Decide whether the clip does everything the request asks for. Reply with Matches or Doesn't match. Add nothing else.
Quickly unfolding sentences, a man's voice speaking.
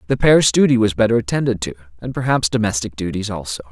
Doesn't match